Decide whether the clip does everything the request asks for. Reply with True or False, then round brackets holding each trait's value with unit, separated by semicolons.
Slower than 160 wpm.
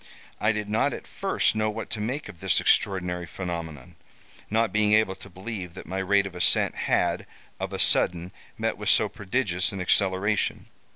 False (180 wpm)